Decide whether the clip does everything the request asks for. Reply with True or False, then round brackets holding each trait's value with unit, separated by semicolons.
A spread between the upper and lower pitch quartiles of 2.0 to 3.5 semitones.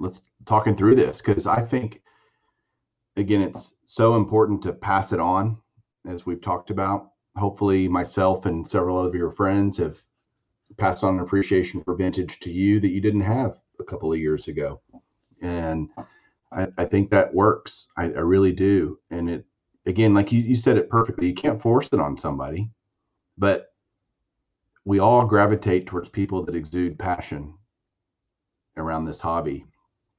True (2.9 semitones)